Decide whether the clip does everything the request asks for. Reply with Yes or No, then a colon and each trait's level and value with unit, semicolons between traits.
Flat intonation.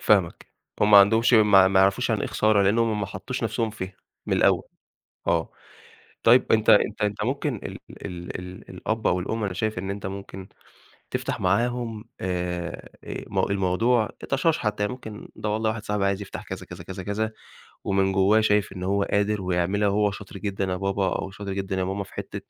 Yes: narrow, 2.3 semitones